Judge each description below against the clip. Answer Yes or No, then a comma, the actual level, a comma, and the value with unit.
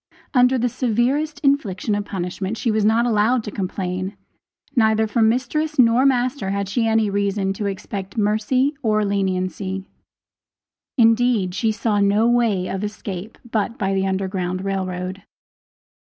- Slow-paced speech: No, average, 145 wpm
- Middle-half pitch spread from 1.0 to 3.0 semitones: No, average, 3.5 semitones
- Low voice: No, high, 210 Hz